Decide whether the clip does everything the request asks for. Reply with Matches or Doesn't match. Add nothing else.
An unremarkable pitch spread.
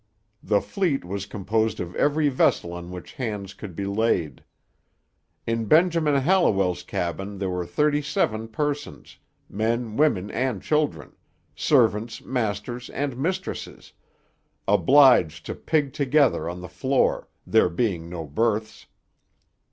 Doesn't match